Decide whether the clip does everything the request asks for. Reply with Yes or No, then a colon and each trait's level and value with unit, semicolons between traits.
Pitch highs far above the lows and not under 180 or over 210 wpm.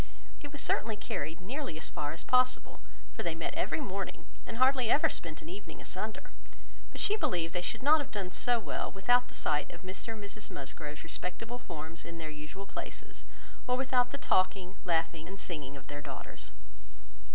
Yes: wide, 7.2 semitones; average, 190 wpm